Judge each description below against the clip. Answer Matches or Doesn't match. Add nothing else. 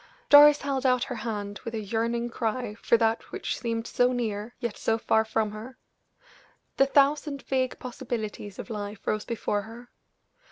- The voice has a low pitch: Doesn't match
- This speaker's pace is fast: Doesn't match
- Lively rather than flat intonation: Doesn't match